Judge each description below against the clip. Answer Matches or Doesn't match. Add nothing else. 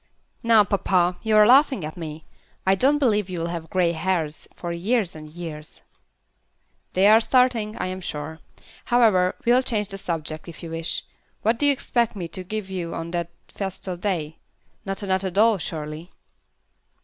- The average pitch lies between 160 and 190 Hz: Matches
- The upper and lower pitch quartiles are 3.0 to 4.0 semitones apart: Doesn't match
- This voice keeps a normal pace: Matches